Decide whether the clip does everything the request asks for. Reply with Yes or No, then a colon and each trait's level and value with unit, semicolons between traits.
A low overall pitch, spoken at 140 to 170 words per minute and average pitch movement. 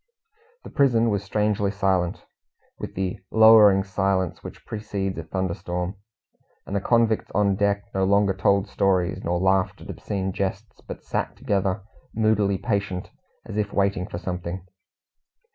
No: low, 100 Hz; average, 145 wpm; narrow, 1.6 semitones